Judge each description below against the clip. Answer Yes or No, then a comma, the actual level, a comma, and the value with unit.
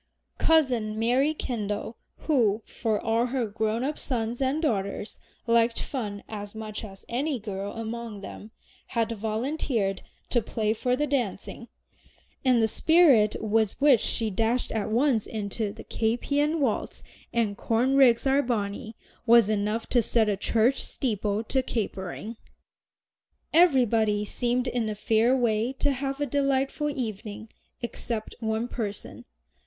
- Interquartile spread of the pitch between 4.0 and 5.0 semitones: No, average, 3.3 semitones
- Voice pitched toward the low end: No, high, 230 Hz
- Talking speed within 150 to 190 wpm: No, average, 140 wpm